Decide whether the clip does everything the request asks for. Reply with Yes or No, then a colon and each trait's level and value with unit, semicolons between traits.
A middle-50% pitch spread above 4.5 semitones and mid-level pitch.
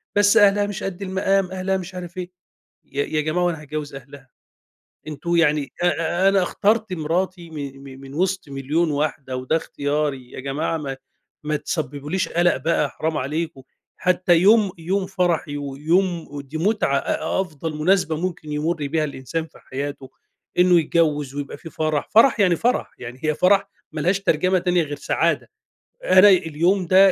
No: average, 4.1 semitones; medium, 165 Hz